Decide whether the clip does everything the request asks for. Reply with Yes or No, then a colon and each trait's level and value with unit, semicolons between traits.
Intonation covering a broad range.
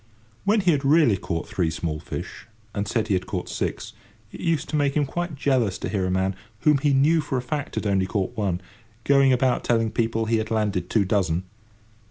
Yes: wide, 6.7 semitones